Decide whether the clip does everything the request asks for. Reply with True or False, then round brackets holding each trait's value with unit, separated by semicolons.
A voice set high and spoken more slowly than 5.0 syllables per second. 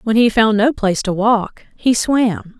True (220 Hz; 4.2 syllables/s)